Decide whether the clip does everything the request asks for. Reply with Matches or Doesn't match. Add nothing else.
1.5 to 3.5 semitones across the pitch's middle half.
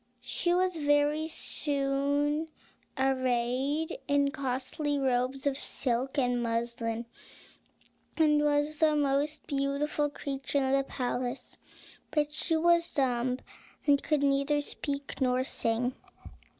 Matches